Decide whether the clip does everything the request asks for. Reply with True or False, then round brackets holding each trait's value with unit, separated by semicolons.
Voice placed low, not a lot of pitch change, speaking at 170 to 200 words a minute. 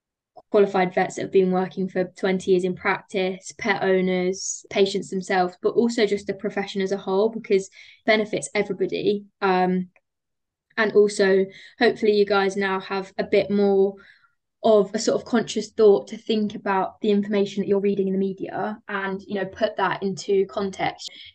False (200 Hz; 1.6 semitones; 175 wpm)